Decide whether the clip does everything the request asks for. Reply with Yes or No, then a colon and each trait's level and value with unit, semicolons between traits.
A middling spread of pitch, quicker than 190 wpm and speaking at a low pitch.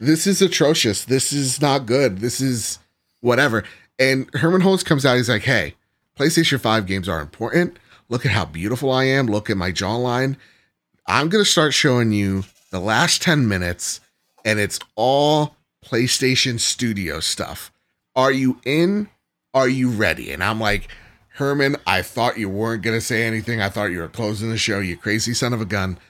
No: average, 4.7 semitones; average, 185 wpm; low, 120 Hz